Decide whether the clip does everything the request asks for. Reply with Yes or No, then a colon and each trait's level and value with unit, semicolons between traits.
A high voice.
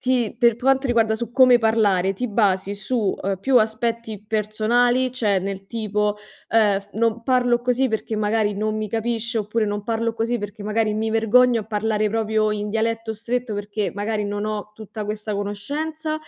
Yes: high, 220 Hz